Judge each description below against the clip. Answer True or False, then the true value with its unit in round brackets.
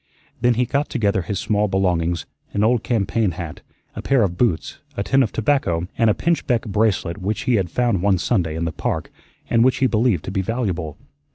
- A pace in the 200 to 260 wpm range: True (205 wpm)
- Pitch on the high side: False (105 Hz)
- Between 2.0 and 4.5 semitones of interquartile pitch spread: False (5.0 semitones)